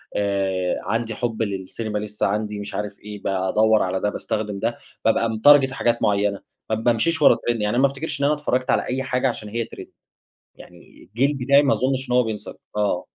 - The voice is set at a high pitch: No, low, 110 Hz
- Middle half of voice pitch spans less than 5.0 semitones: Yes, average, 3.7 semitones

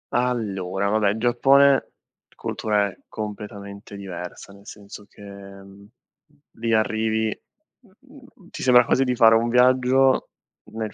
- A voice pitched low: Yes, low, 110 Hz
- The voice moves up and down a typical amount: Yes, average, 3.8 semitones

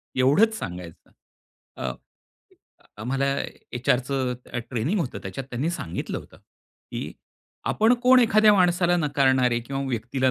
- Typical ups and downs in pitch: No, wide, 6.2 semitones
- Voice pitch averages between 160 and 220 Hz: No, low, 135 Hz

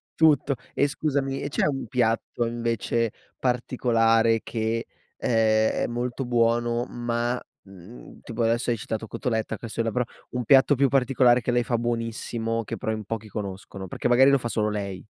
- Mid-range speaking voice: No, low, 115 Hz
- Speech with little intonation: Yes, narrow, 1.8 semitones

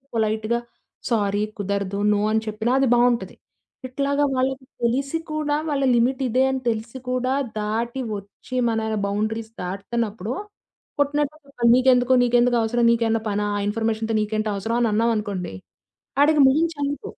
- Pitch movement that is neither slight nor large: Yes, average, 3.3 semitones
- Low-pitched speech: No, high, 235 Hz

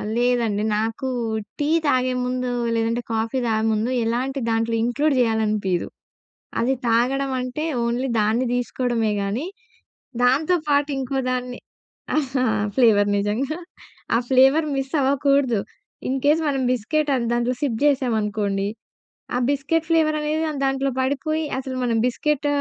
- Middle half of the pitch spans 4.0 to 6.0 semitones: No, average, 3.3 semitones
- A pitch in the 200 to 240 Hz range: No, very high, 255 Hz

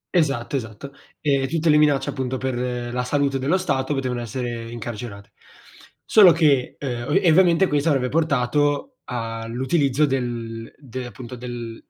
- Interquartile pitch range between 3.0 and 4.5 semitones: Yes, average, 3.4 semitones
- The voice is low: Yes, low, 130 Hz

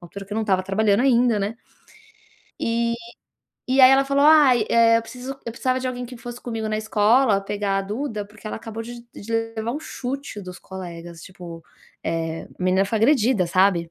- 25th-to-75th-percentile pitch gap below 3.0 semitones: No, average, 3.9 semitones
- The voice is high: Yes, high, 220 Hz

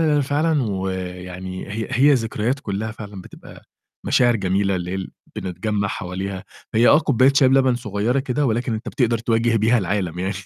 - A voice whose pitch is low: Yes, low, 110 Hz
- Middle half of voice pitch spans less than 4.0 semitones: No, average, 4.6 semitones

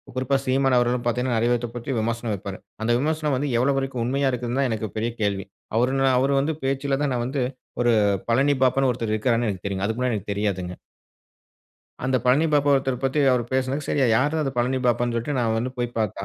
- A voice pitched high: No, low, 125 Hz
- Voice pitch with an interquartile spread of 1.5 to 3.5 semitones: Yes, average, 2.7 semitones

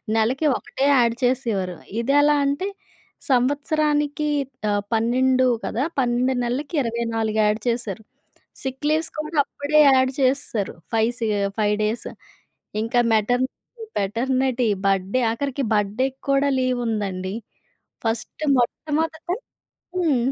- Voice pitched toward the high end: Yes, very high, 250 Hz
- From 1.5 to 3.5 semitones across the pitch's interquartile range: No, average, 3.9 semitones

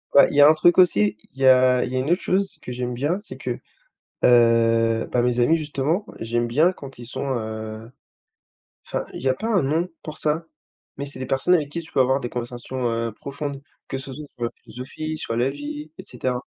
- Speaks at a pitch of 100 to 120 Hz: No, low, 130 Hz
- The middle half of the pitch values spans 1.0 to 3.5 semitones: No, average, 4.0 semitones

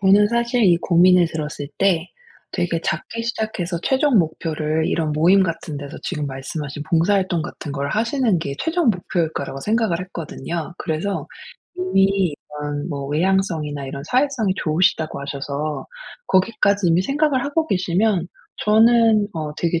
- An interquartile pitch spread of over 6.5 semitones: No, wide, 5.5 semitones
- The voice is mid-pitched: Yes, medium, 175 Hz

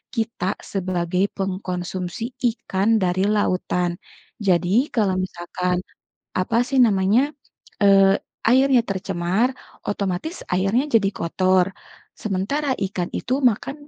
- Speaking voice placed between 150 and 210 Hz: Yes, high, 190 Hz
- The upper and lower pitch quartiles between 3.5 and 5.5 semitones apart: No, average, 3.1 semitones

